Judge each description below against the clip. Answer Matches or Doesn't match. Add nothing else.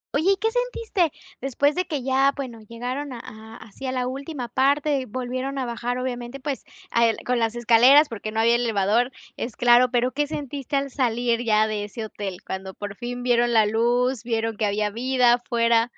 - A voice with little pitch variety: Doesn't match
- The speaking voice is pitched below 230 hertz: Doesn't match